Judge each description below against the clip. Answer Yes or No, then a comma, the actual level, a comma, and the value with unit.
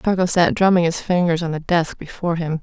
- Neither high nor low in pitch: Yes, medium, 170 Hz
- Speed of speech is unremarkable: No, fast, 230 wpm